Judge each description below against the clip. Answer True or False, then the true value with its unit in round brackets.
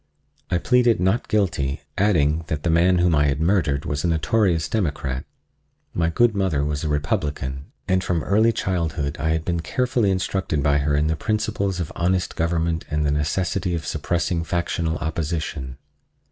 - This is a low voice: True (85 Hz)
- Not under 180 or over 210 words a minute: False (170 wpm)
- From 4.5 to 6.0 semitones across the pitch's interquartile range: False (3.9 semitones)